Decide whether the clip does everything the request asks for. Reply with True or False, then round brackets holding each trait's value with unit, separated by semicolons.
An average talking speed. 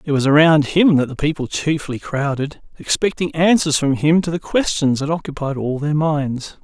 True (190 wpm)